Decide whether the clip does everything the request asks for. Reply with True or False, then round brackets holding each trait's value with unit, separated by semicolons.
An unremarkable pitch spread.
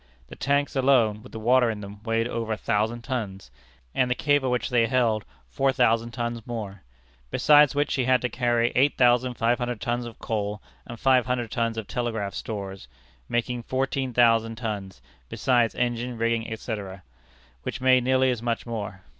False (2.1 semitones)